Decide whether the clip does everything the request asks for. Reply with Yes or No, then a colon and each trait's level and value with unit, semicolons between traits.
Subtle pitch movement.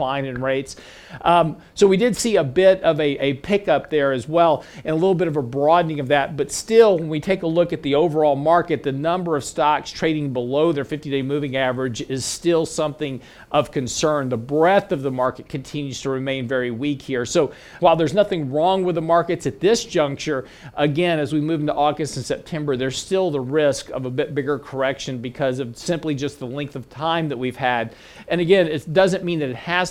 No: average, 3.8 semitones